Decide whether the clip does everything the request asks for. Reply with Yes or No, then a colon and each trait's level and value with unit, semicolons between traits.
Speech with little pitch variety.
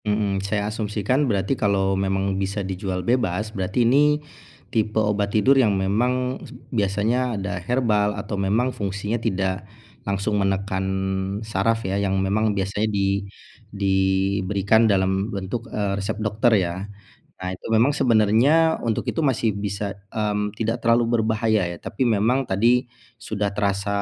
Yes: narrow, 2.2 semitones